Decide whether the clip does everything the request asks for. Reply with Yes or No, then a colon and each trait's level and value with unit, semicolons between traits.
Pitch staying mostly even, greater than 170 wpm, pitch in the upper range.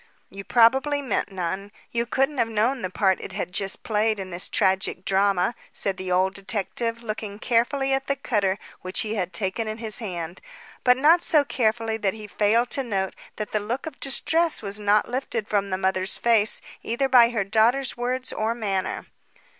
No: average, 3.9 semitones; average, 190 wpm; high, 215 Hz